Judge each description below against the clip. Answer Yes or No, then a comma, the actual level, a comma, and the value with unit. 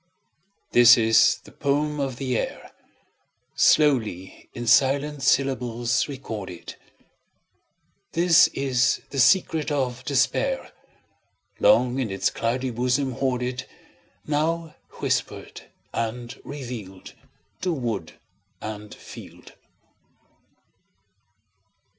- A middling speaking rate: No, slow, 85 wpm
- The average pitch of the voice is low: Yes, low, 130 Hz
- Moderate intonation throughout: Yes, average, 3.3 semitones